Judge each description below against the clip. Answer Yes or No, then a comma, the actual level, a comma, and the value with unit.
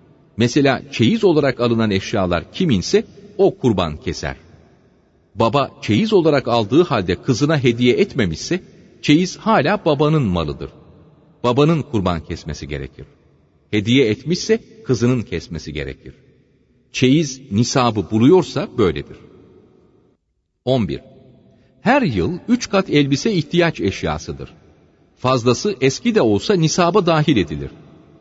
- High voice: No, low, 135 Hz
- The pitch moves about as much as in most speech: No, wide, 8.3 semitones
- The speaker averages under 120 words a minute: Yes, average, 105 wpm